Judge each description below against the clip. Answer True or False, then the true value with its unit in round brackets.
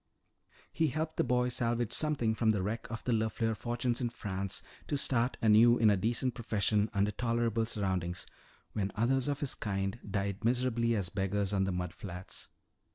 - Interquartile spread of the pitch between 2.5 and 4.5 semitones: True (3.3 semitones)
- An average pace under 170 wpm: False (175 wpm)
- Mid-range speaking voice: False (110 Hz)